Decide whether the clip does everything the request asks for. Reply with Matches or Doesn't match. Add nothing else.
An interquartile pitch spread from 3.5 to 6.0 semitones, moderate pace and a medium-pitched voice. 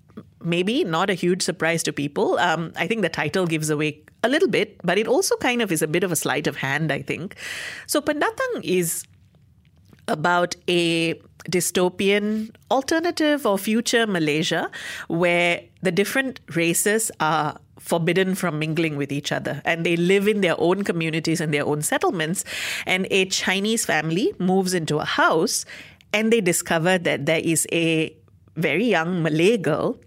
Matches